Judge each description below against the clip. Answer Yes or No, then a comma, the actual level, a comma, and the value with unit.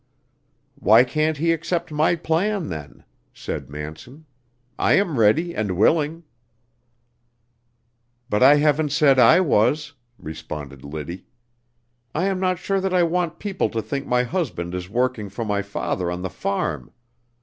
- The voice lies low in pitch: Yes, low, 130 Hz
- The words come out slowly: No, average, 145 wpm